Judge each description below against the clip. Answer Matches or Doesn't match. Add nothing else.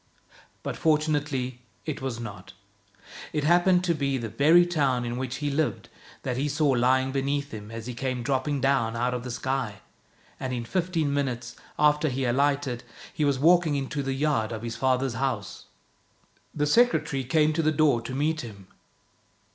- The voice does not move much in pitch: Doesn't match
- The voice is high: Doesn't match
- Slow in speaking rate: Doesn't match